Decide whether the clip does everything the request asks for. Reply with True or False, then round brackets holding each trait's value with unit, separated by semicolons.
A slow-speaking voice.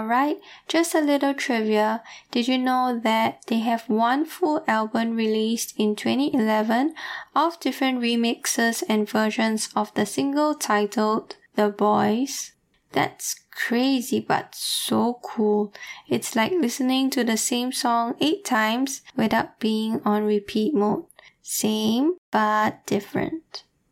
True (125 wpm)